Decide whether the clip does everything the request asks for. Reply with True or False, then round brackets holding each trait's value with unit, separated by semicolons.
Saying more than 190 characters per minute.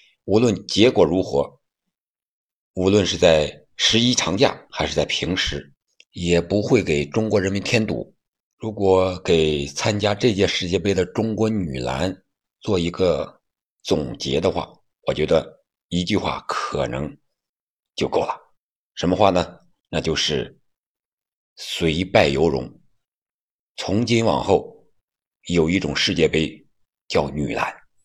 False (185 characters per minute)